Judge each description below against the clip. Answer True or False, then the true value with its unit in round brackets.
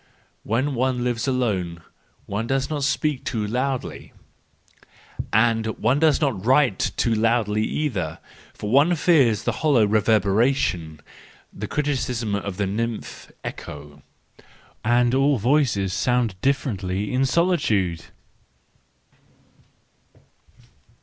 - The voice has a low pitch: True (120 Hz)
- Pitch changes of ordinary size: True (4.6 semitones)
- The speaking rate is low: True (105 wpm)